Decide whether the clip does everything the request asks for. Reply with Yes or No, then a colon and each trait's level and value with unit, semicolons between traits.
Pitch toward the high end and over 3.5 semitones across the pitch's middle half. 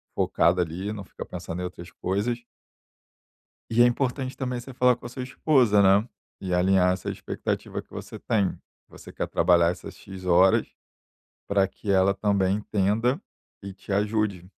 No: low, 100 Hz; average, 4.3 semitones